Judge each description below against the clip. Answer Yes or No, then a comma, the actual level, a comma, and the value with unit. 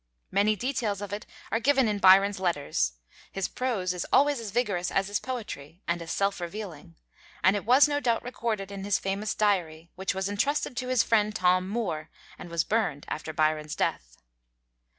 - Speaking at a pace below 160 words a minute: No, average, 185 wpm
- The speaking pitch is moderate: No, high, 200 Hz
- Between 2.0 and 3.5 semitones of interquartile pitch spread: No, average, 4.4 semitones